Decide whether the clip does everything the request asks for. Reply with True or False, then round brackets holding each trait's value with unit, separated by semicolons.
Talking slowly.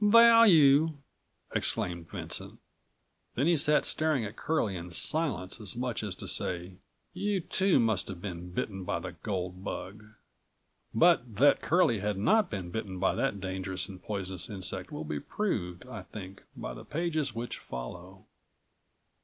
False (155 wpm)